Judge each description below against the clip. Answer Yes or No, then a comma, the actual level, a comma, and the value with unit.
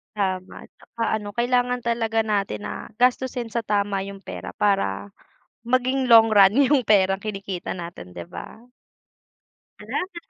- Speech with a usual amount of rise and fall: Yes, average, 3.7 semitones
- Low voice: No, high, 210 Hz